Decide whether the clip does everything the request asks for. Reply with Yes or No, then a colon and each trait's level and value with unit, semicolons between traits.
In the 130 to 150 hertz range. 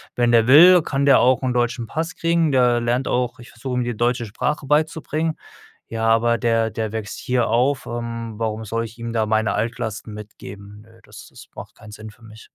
No: low, 120 Hz